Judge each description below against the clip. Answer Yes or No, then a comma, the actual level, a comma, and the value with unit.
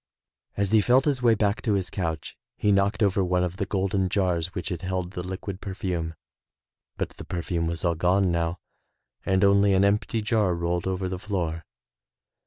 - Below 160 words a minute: No, average, 190 wpm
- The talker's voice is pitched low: Yes, very low, 95 Hz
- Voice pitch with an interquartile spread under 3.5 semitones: Yes, narrow, 2.4 semitones